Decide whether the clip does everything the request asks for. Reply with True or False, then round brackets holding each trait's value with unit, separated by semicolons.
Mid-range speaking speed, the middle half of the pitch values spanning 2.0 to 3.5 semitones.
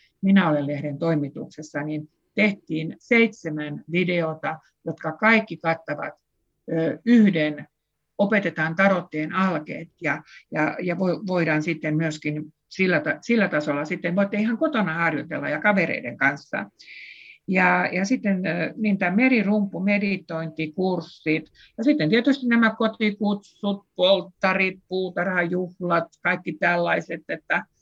False (110 wpm; 4.1 semitones)